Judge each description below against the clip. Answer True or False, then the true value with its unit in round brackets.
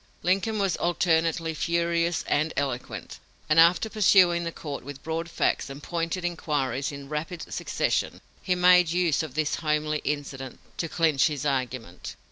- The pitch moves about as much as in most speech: True (3.2 semitones)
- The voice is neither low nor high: True (160 Hz)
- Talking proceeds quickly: False (150 wpm)